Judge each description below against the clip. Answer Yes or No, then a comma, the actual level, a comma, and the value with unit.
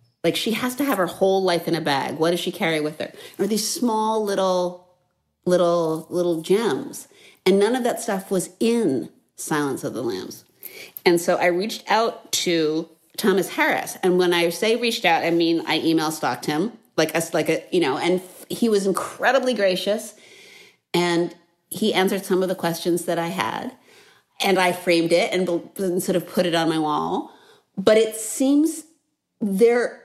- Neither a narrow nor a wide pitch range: Yes, average, 4.2 semitones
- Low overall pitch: No, medium, 180 Hz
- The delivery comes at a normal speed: Yes, average, 185 wpm